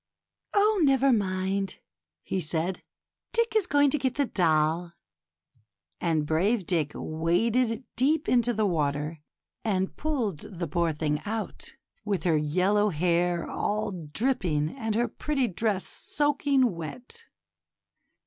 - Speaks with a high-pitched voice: Yes, high, 195 Hz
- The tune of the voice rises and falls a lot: Yes, wide, 7.5 semitones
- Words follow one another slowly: Yes, slow, 130 wpm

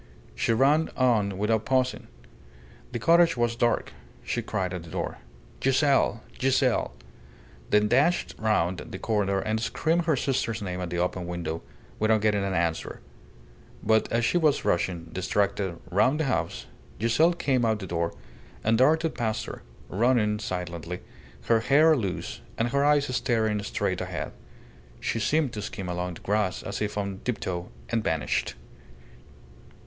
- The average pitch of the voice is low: Yes, low, 110 Hz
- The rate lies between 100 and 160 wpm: Yes, average, 155 wpm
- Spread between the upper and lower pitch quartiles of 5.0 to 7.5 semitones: Yes, wide, 5.5 semitones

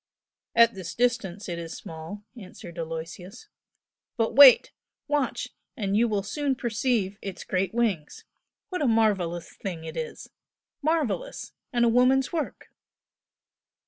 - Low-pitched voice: No, high, 210 Hz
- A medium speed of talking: No, slow, 130 wpm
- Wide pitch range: Yes, wide, 5.9 semitones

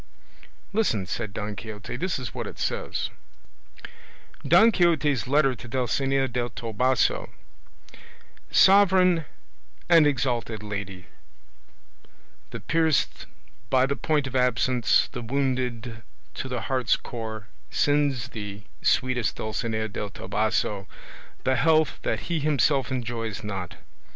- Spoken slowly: Yes, slow, 115 wpm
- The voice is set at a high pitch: No, low, 125 Hz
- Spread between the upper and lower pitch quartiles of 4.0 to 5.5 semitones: Yes, average, 4.8 semitones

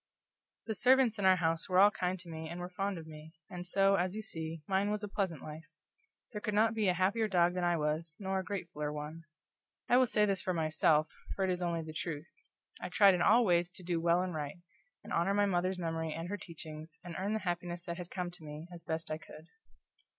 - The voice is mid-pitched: Yes, medium, 175 Hz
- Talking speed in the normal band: No, fast, 245 wpm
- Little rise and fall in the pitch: No, average, 3.1 semitones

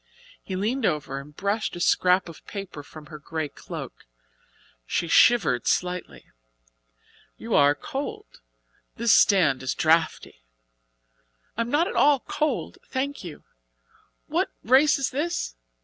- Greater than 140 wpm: No, slow, 135 wpm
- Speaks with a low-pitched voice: No, medium, 180 Hz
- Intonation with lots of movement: Yes, wide, 8.8 semitones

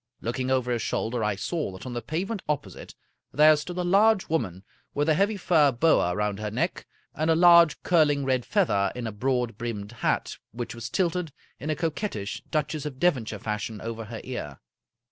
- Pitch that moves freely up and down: Yes, wide, 6.5 semitones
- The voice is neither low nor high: No, low, 130 Hz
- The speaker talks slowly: No, average, 195 wpm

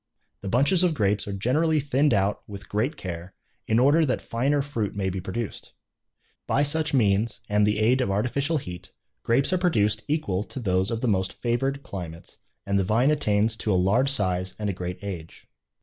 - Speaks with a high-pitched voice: No, low, 110 Hz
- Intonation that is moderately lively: No, wide, 5.9 semitones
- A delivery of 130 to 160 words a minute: No, average, 195 wpm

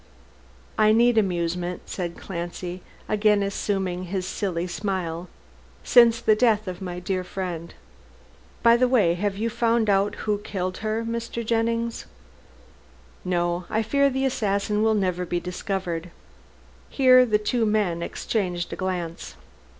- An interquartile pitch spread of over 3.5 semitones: Yes, average, 3.9 semitones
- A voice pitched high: Yes, high, 200 Hz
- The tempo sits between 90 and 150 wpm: Yes, slow, 135 wpm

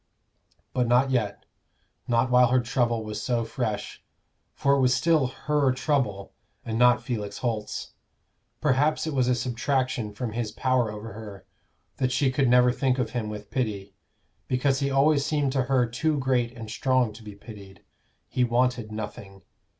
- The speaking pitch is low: Yes, low, 125 Hz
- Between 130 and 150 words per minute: No, average, 165 wpm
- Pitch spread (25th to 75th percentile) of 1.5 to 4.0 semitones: Yes, average, 3.1 semitones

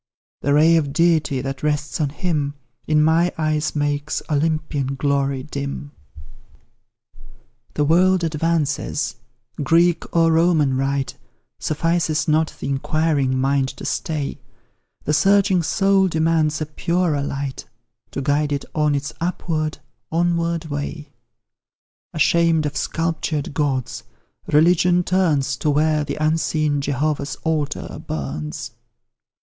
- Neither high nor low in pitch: Yes, medium, 150 Hz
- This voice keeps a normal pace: No, slow, 115 wpm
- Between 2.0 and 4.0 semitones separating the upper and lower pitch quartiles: Yes, narrow, 2.6 semitones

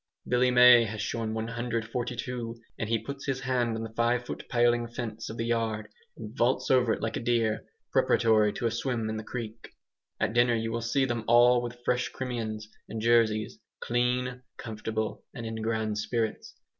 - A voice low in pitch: Yes, low, 115 Hz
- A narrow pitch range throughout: Yes, narrow, 1.7 semitones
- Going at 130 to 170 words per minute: No, average, 180 wpm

